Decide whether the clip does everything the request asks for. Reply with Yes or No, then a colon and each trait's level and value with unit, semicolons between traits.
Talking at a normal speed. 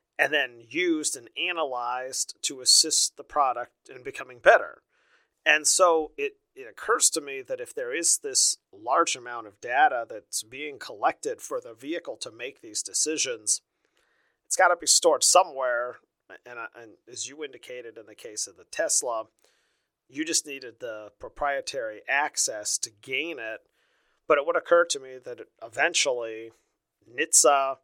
Yes: average, 155 wpm